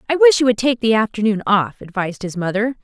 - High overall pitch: Yes, high, 220 Hz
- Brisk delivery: Yes, fast, 235 wpm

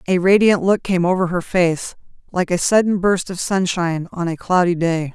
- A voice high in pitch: No, medium, 180 Hz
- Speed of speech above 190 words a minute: Yes, average, 200 wpm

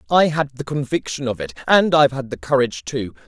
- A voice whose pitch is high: No, low, 135 Hz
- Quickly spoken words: Yes, fast, 220 wpm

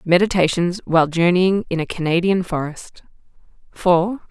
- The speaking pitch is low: No, medium, 175 Hz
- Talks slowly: Yes, slow, 110 wpm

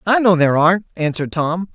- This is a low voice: No, medium, 175 Hz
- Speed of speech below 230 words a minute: Yes, fast, 205 wpm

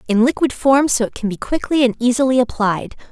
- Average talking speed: No, fast, 210 wpm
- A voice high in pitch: Yes, very high, 250 Hz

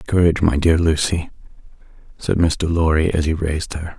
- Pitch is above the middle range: No, very low, 80 Hz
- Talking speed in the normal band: Yes, average, 165 wpm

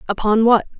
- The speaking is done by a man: No, female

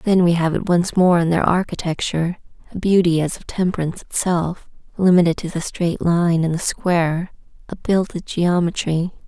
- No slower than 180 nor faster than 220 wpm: No, average, 160 wpm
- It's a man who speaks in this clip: No, female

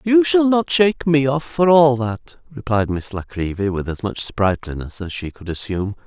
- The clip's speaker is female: No, male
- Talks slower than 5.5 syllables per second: Yes, 4.9 syllables/s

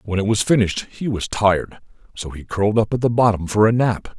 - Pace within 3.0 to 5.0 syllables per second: No, 5.9 syllables/s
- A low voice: Yes, low, 105 Hz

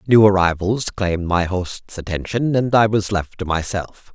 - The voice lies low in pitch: Yes, low, 100 Hz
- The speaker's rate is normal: Yes, average, 175 wpm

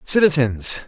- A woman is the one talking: No, male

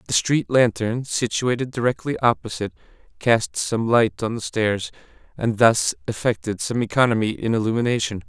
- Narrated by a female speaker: No, male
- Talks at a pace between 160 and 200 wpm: No, average, 140 wpm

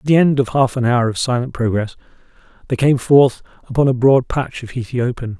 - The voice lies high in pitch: No, low, 125 Hz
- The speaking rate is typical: No, fast, 220 wpm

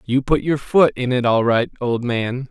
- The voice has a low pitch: Yes, low, 125 Hz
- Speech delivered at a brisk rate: Yes, fast, 240 wpm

